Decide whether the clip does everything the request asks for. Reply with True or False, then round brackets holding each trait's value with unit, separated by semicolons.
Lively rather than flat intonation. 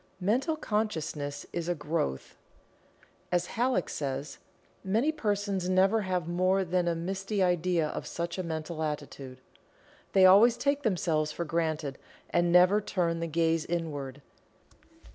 False (3.6 semitones)